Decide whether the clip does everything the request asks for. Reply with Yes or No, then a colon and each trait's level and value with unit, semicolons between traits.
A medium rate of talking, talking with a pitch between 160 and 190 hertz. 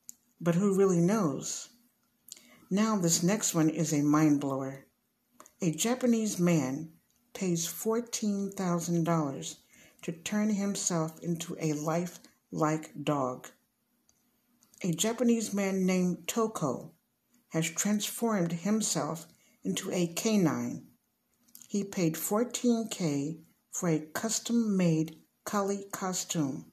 No: slow, 105 wpm; medium, 185 Hz